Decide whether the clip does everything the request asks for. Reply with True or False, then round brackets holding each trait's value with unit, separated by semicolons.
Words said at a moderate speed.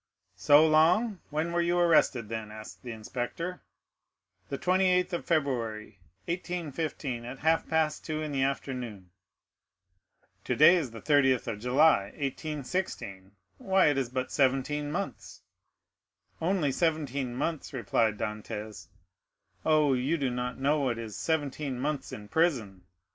False (125 wpm)